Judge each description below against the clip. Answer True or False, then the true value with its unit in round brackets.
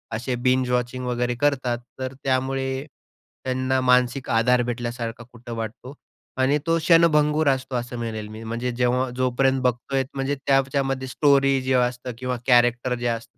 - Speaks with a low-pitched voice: True (125 Hz)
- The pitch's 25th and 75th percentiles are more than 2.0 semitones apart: False (1.7 semitones)